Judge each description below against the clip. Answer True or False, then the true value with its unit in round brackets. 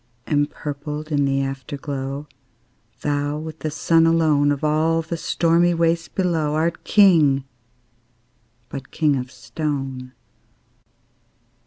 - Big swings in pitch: False (2.7 semitones)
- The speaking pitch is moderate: True (150 Hz)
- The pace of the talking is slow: True (110 wpm)